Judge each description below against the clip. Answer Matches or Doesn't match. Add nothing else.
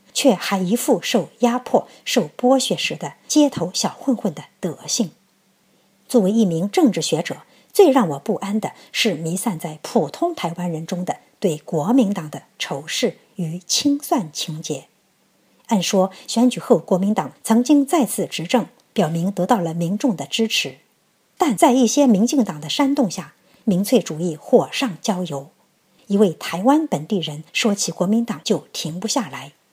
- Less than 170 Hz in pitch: Doesn't match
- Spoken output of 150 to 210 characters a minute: Doesn't match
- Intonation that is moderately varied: Doesn't match